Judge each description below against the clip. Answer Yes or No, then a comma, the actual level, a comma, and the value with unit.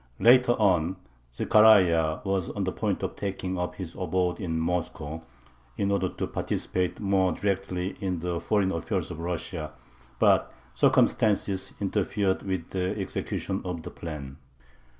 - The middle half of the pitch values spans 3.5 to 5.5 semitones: No, average, 2.7 semitones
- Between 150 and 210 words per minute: No, average, 140 wpm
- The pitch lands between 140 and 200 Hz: No, very low, 90 Hz